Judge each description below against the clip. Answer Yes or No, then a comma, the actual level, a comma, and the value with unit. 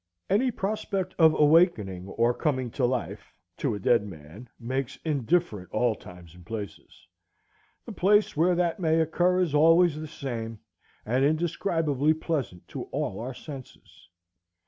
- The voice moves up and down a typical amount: No, wide, 6.7 semitones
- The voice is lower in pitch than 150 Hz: Yes, medium, 140 Hz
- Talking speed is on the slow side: No, average, 145 wpm